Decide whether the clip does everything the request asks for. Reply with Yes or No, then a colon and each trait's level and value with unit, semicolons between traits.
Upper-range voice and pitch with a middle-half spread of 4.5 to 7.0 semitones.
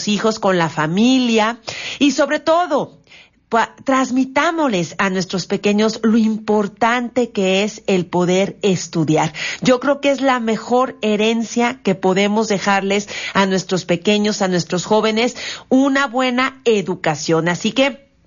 Yes: high, 215 Hz; average, 4.8 semitones